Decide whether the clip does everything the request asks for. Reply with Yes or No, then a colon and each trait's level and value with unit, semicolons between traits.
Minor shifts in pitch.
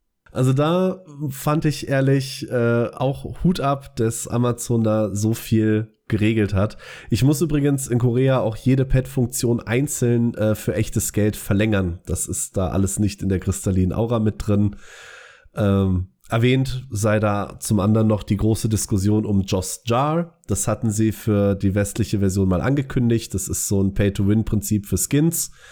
No: average, 4.0 semitones